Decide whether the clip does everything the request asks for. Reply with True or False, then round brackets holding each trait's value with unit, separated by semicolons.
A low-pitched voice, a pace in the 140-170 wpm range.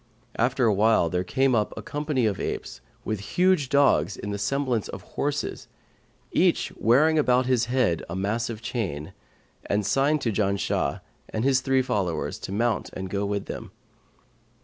True (115 Hz; 160 wpm)